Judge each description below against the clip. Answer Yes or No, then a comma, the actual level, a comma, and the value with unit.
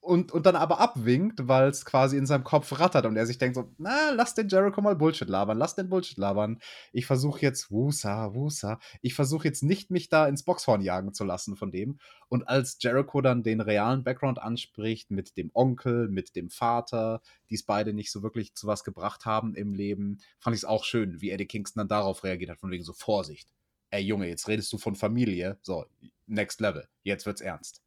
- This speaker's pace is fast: Yes, fast, 215 wpm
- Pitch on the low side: Yes, low, 115 Hz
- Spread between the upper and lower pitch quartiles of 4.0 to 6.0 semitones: Yes, average, 5.1 semitones